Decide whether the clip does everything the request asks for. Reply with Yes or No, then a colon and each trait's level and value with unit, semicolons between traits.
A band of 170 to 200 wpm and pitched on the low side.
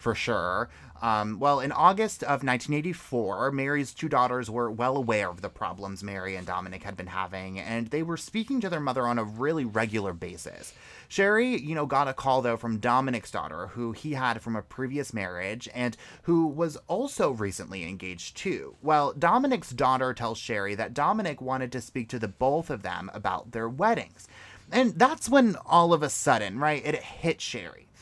Yes: average, 190 wpm; low, 130 Hz